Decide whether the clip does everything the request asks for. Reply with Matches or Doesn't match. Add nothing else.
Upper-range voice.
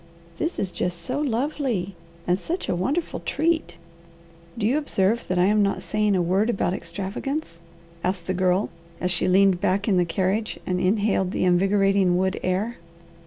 Matches